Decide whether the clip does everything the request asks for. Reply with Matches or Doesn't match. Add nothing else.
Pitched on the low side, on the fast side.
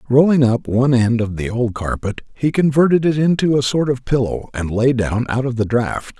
Matches